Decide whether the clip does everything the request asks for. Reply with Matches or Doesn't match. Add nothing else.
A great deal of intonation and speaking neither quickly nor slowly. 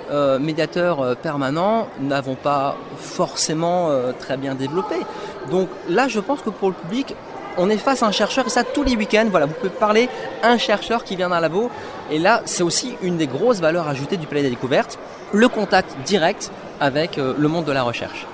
Matches